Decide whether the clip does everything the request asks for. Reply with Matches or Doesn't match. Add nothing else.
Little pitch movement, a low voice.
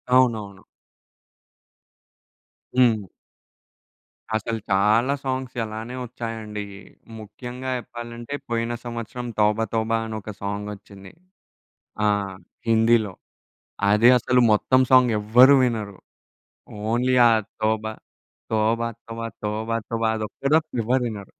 Matches